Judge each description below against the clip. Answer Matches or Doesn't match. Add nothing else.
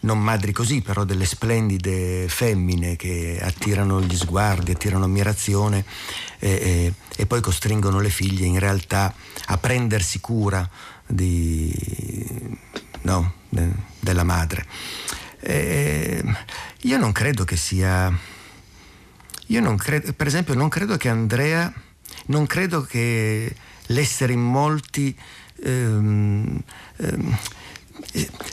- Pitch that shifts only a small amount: Doesn't match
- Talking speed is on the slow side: Matches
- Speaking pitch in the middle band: Doesn't match